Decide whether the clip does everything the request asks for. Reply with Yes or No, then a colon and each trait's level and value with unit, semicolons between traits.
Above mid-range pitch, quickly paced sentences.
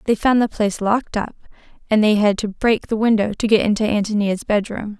Yes: high, 215 Hz; fast, 215 wpm